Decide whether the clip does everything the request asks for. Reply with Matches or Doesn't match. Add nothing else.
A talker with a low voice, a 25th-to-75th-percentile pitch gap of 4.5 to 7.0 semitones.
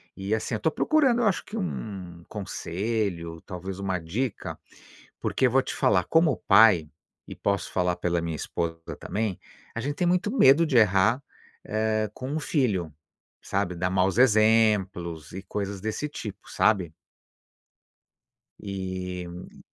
Matches